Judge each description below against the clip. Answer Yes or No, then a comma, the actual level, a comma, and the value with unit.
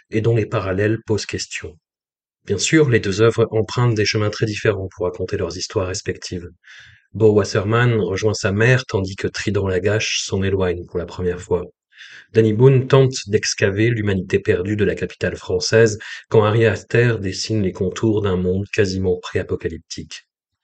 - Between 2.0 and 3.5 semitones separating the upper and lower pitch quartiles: Yes, average, 3.0 semitones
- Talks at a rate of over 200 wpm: No, average, 165 wpm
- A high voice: No, low, 105 Hz